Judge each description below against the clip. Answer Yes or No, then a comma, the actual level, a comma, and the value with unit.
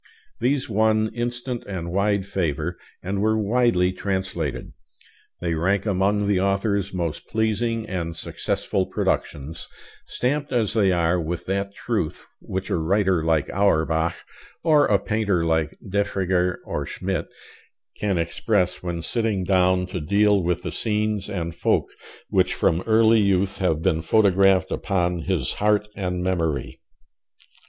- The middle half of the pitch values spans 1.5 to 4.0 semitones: Yes, average, 3.2 semitones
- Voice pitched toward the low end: Yes, very low, 95 Hz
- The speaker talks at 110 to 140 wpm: Yes, slow, 135 wpm